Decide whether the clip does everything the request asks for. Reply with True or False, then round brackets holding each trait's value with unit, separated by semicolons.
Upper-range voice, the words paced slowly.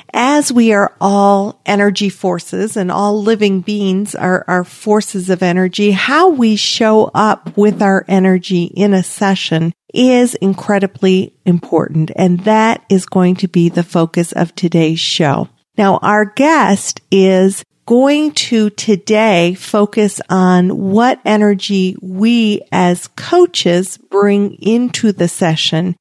True (195 Hz; 130 wpm)